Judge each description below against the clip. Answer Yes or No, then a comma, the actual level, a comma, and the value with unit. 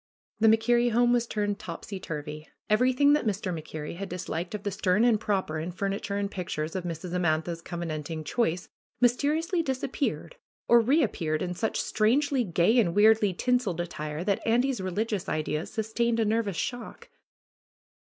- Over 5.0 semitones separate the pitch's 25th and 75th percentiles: Yes, wide, 5.6 semitones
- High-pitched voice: Yes, high, 205 Hz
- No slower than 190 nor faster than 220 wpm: No, average, 160 wpm